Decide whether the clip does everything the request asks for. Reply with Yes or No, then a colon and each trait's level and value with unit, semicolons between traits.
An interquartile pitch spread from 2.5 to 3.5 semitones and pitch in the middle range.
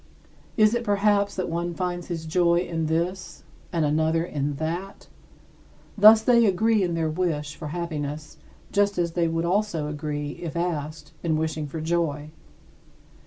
Yes: average, 3.0 semitones; medium, 170 Hz